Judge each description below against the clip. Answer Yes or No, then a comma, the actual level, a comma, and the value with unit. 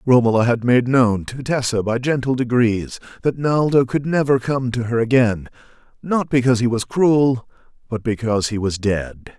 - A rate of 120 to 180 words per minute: Yes, average, 175 wpm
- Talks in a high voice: No, low, 120 Hz